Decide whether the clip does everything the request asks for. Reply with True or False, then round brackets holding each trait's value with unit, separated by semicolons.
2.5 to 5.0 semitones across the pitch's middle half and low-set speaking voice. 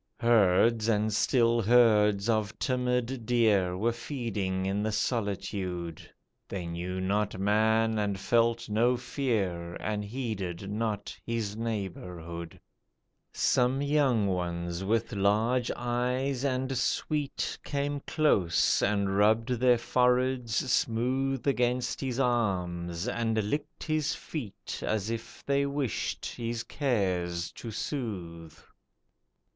True (4.2 semitones; 115 Hz)